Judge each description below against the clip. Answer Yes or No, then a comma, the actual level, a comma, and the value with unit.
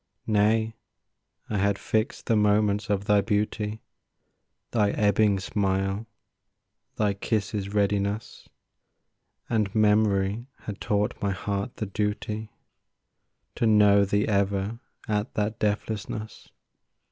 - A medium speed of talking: No, slow, 105 wpm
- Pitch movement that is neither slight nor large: No, narrow, 1.2 semitones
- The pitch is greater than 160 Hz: No, low, 105 Hz